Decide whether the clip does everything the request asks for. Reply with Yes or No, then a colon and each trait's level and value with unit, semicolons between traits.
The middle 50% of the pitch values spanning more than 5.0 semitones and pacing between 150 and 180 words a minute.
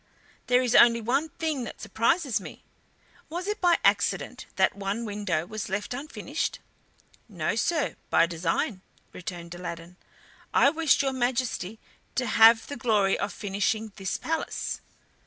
No: wide, 5.5 semitones; average, 140 wpm